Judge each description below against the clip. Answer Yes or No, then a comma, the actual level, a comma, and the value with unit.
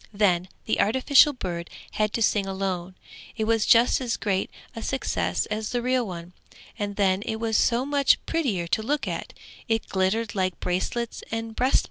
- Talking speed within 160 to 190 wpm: Yes, average, 180 wpm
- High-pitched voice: Yes, high, 220 Hz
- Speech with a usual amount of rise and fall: Yes, average, 4.0 semitones